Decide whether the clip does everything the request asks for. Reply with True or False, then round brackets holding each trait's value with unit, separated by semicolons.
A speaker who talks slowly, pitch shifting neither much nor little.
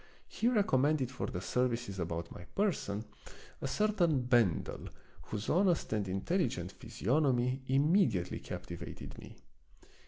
False (120 wpm; 8.2 semitones)